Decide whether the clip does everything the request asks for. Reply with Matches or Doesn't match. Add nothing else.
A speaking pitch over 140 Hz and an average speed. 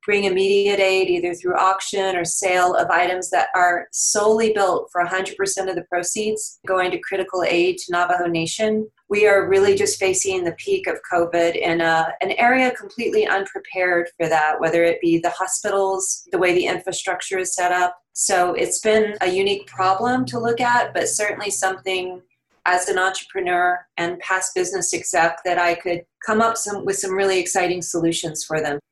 Matches